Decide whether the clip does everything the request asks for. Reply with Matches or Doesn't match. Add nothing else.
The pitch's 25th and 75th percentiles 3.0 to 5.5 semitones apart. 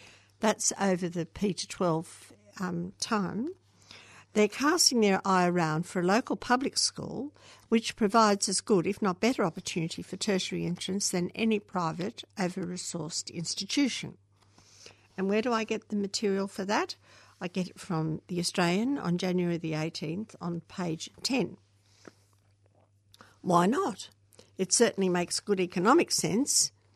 Matches